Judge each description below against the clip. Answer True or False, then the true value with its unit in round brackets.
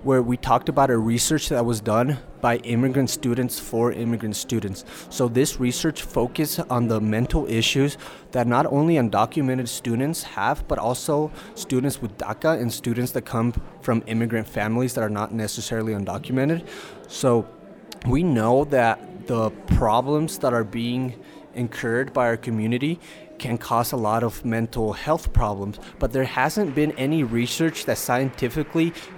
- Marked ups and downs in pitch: False (3.5 semitones)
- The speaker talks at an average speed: True (155 wpm)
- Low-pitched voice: True (125 Hz)